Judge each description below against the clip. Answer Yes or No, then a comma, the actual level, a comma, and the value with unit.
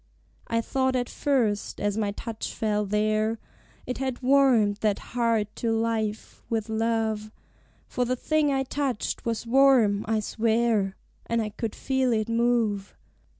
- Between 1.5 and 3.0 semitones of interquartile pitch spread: Yes, narrow, 2.6 semitones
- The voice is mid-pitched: No, high, 225 Hz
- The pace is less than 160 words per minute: Yes, average, 150 wpm